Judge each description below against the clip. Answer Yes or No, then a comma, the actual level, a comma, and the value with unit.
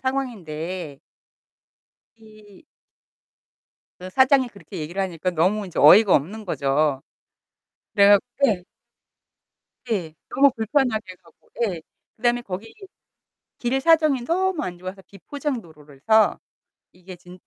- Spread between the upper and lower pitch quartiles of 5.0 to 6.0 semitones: Yes, wide, 5.6 semitones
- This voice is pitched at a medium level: No, high, 200 Hz